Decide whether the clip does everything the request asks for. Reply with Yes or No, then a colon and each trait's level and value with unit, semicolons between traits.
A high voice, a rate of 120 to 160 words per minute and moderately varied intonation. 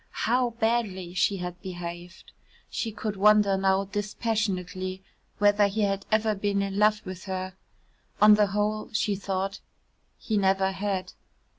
No: high, 200 Hz; average, 140 wpm; narrow, 2.0 semitones